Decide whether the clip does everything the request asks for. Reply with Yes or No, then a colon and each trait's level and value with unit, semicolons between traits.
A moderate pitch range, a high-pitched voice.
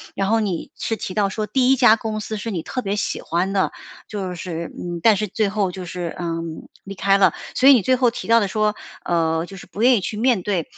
Yes: average, 3.7 semitones; high, 200 Hz